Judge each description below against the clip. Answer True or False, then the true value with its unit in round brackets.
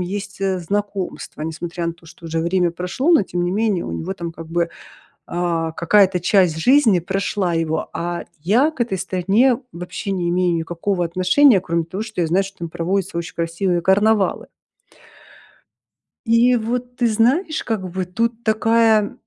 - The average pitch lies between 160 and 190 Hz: True (185 Hz)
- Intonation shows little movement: False (4.2 semitones)